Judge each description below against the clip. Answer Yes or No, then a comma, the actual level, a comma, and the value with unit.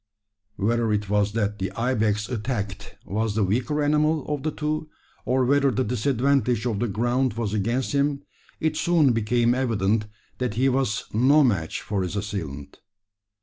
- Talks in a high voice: No, low, 120 Hz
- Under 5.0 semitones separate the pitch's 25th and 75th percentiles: Yes, average, 4.4 semitones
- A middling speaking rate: Yes, average, 160 wpm